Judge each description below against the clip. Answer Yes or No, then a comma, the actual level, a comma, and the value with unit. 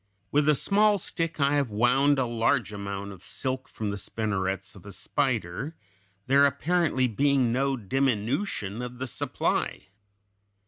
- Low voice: Yes, low, 125 Hz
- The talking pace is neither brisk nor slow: Yes, average, 145 wpm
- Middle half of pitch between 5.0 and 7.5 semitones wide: Yes, wide, 5.5 semitones